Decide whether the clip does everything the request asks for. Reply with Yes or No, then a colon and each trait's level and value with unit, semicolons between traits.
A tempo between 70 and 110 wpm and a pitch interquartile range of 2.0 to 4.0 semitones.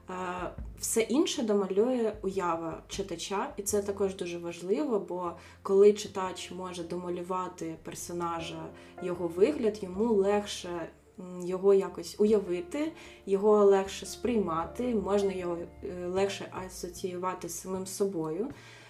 Yes: slow, 105 wpm; narrow, 2.5 semitones